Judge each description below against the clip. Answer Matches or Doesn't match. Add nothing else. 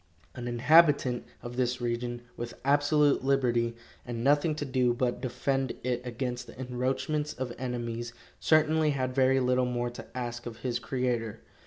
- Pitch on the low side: Matches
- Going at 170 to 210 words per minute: Doesn't match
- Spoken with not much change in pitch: Matches